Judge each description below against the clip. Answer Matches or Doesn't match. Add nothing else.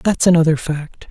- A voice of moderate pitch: Matches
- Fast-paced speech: Doesn't match